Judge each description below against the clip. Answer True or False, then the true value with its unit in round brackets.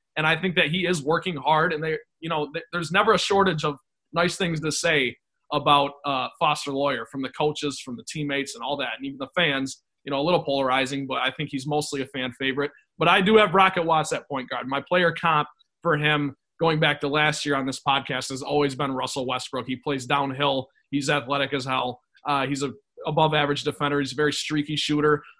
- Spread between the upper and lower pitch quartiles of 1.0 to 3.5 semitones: True (2.4 semitones)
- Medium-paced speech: False (225 wpm)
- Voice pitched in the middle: True (145 Hz)